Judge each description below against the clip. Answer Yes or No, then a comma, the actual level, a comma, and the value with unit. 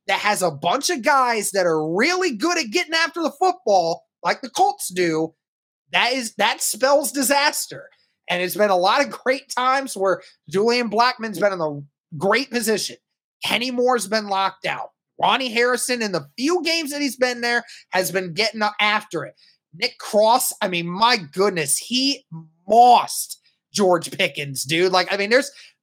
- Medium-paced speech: Yes, average, 175 wpm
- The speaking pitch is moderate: No, high, 220 Hz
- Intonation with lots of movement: Yes, wide, 6.2 semitones